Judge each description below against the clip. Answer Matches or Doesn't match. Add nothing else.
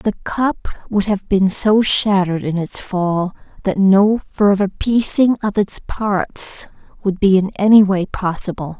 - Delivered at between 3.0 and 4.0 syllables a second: Matches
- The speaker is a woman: Matches